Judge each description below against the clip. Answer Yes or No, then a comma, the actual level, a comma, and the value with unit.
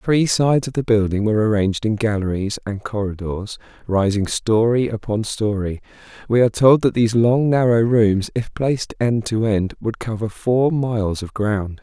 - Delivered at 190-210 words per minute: No, average, 175 wpm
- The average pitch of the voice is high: No, low, 110 Hz